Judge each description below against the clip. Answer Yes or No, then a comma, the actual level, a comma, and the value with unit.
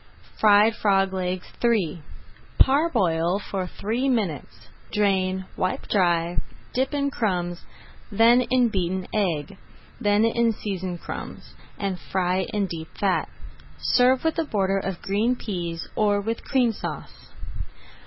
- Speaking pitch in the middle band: No, high, 200 Hz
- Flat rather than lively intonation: No, average, 3.8 semitones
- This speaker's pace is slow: Yes, slow, 125 wpm